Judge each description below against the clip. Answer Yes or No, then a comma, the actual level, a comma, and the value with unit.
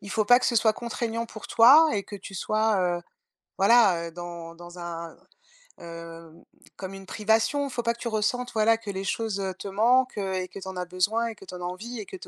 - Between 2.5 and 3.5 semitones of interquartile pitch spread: No, average, 4.1 semitones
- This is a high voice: Yes, high, 205 Hz